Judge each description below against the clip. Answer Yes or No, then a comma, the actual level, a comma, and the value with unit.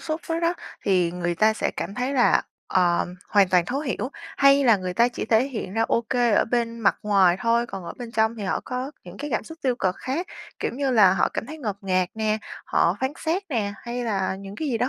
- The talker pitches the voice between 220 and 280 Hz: Yes, high, 225 Hz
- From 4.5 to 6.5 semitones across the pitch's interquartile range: Yes, average, 5.0 semitones